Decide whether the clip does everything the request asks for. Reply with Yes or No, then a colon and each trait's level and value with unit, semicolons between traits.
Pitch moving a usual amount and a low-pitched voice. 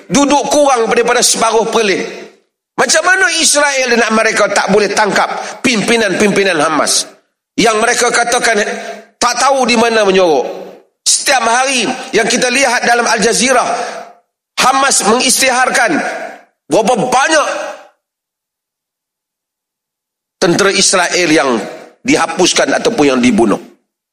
No: average, 3.3 semitones; high, 235 Hz